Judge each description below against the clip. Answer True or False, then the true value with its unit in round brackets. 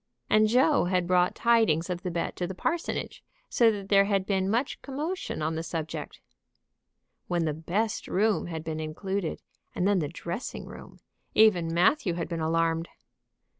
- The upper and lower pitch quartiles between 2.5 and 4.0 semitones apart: False (4.4 semitones)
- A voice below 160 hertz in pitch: False (180 Hz)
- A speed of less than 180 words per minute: True (170 wpm)